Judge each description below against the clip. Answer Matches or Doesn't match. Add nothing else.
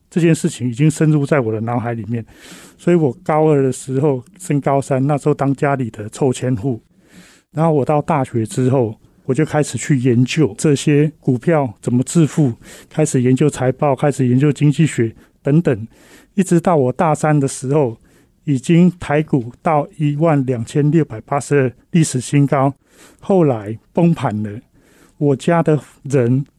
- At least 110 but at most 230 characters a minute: Doesn't match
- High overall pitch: Doesn't match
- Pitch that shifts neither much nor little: Matches